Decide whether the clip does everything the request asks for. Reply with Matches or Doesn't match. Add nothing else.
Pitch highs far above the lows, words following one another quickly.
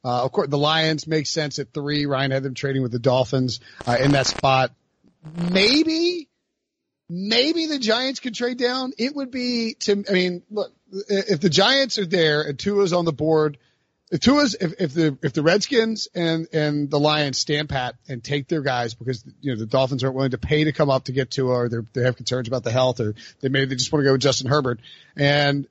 Matches